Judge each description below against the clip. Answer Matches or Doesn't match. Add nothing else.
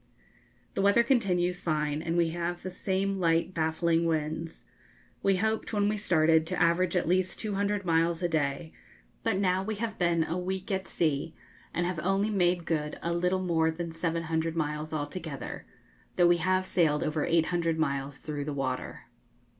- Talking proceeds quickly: Doesn't match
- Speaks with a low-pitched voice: Doesn't match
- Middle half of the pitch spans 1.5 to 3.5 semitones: Matches